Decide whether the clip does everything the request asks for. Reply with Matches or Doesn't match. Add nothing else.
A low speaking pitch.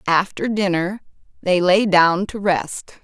Doesn't match